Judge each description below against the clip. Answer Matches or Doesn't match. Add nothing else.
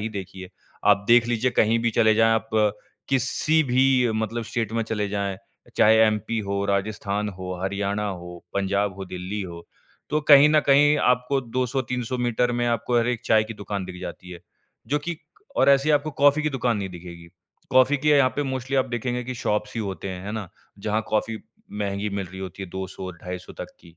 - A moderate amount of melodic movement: Matches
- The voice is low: Matches